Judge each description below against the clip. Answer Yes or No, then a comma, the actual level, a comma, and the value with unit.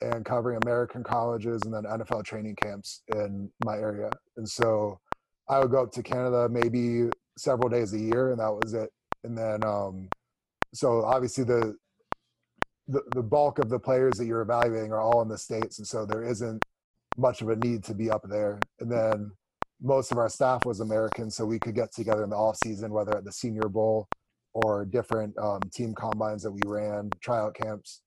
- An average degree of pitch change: No, narrow, 2.1 semitones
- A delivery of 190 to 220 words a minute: Yes, average, 200 wpm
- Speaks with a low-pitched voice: Yes, low, 110 Hz